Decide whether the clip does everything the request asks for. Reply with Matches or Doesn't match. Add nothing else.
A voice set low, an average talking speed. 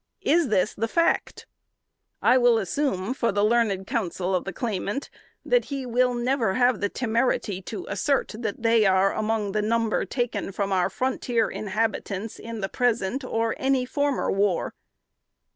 Doesn't match